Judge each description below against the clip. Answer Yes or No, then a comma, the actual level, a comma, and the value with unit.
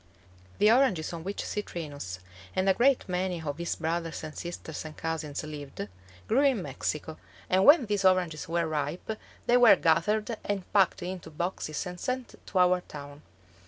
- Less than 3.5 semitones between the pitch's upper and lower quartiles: No, average, 4.4 semitones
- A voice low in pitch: No, medium, 175 Hz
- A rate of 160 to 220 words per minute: Yes, average, 165 wpm